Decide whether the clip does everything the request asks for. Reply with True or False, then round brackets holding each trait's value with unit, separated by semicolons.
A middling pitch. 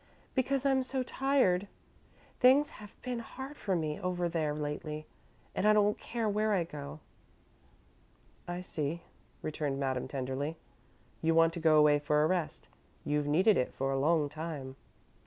True (165 Hz)